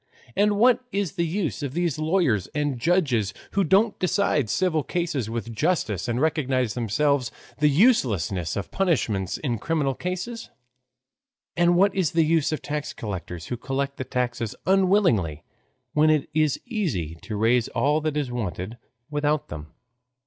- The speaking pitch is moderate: Yes, medium, 145 Hz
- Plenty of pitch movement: Yes, wide, 7.0 semitones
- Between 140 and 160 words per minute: Yes, average, 155 wpm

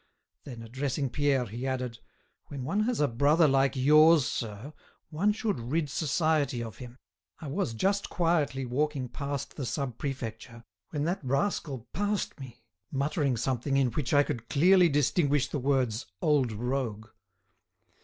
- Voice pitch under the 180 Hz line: Yes, medium, 140 Hz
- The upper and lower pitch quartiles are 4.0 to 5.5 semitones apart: No, average, 3.6 semitones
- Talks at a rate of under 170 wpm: Yes, average, 150 wpm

